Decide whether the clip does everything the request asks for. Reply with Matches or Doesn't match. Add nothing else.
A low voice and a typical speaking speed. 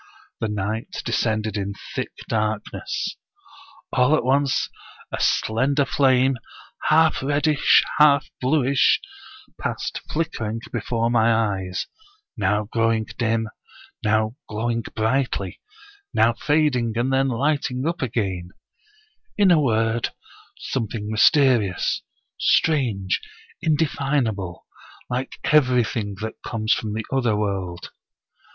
Doesn't match